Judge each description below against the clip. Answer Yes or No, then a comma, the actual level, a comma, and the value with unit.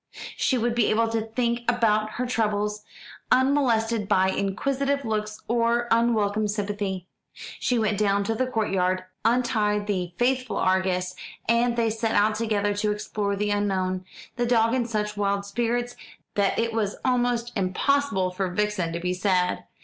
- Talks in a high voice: Yes, high, 215 Hz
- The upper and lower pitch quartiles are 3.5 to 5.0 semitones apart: No, average, 2.8 semitones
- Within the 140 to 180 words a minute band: Yes, average, 155 wpm